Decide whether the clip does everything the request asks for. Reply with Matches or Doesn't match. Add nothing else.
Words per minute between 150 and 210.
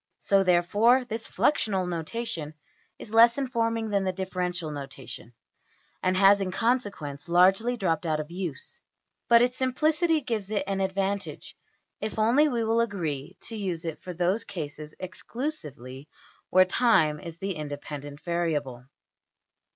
Doesn't match